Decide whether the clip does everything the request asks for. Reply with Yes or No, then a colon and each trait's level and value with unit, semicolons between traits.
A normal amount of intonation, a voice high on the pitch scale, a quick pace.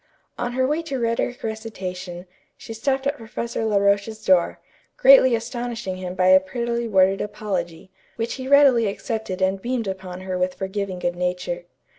No: average, 4.1 semitones; high, 210 Hz; average, 165 wpm